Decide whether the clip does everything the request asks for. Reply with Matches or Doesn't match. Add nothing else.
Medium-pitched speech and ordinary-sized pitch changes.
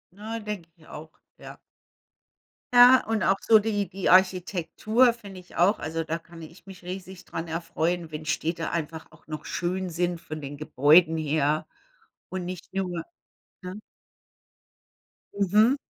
Matches